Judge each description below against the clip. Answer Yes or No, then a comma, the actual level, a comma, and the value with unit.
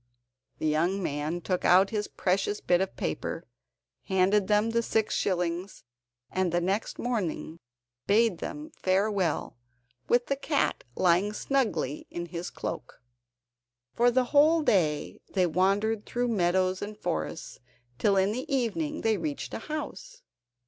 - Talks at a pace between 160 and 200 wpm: No, average, 140 wpm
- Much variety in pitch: No, average, 4.8 semitones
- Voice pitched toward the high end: Yes, high, 200 Hz